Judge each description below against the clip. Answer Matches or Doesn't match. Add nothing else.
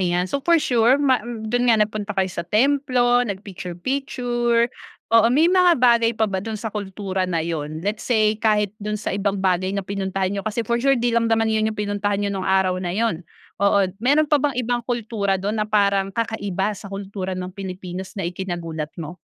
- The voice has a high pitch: Matches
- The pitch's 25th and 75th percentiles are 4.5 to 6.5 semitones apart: Doesn't match